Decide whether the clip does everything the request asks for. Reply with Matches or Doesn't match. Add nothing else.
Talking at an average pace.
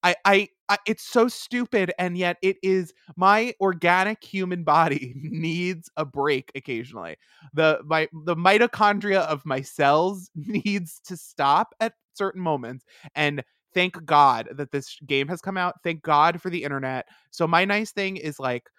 Matches